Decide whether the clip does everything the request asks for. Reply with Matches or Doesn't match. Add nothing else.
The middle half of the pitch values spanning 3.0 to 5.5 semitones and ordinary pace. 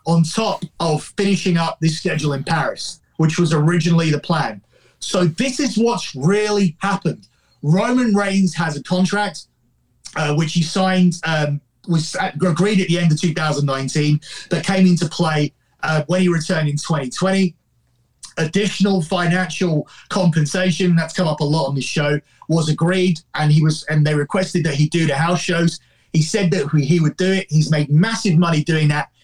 Matches